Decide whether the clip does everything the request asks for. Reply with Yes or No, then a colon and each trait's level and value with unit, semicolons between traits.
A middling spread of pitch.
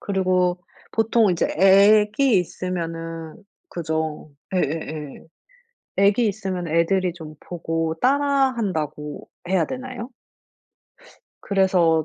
Yes: average, 4.2 semitones